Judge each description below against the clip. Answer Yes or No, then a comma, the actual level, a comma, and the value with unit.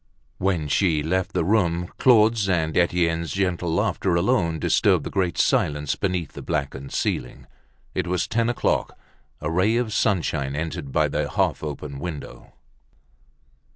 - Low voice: Yes, very low, 85 Hz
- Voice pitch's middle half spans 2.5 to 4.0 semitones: Yes, average, 3.7 semitones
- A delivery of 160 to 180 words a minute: No, average, 145 wpm